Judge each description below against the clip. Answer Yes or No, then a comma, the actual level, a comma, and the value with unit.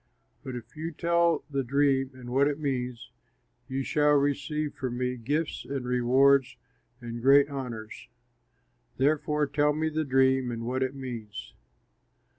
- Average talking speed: Yes, average, 145 wpm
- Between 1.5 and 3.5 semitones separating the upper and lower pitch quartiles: Yes, average, 2.7 semitones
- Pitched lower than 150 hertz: Yes, low, 135 Hz